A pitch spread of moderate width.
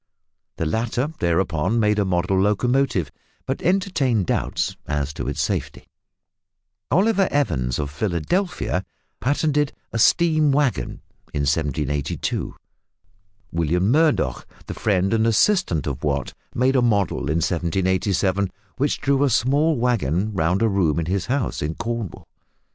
No: wide, 8.4 semitones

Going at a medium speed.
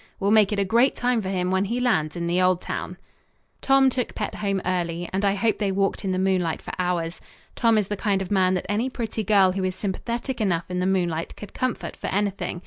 No: fast, 240 wpm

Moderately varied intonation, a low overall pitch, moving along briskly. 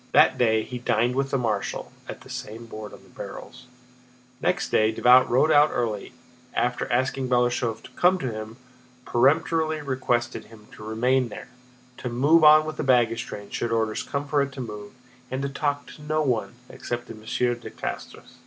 No: average, 3.6 semitones; low, 125 Hz; average, 190 wpm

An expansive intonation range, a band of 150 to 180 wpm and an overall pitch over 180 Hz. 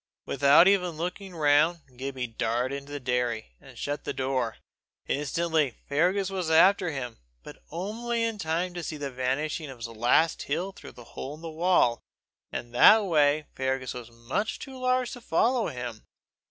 No: wide, 5.9 semitones; average, 170 wpm; medium, 150 Hz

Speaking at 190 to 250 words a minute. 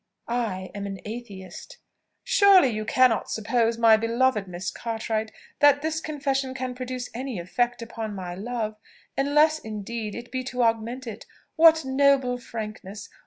No: average, 145 wpm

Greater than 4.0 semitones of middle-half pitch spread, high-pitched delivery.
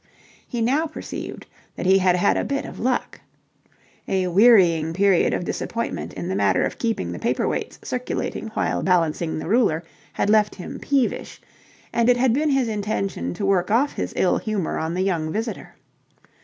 Yes: average, 5.1 semitones; high, 200 Hz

